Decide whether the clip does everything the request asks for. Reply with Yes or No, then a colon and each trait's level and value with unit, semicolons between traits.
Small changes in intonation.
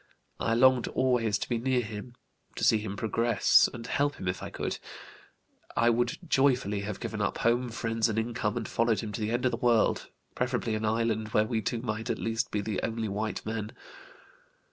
Yes: narrow, 2.0 semitones